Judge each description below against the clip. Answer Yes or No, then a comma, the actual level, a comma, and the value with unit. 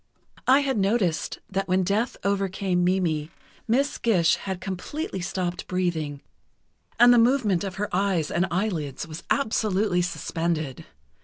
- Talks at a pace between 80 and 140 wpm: Yes, slow, 135 wpm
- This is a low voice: No, high, 190 Hz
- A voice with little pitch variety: No, average, 3.5 semitones